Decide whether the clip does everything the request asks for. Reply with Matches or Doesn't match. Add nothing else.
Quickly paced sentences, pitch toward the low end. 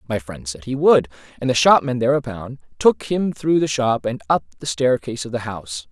Matches